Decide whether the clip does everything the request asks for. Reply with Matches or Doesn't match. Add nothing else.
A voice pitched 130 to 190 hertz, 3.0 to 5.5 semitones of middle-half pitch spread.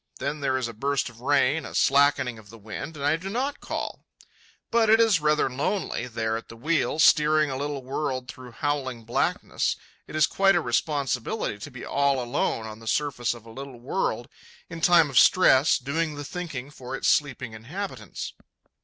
Matches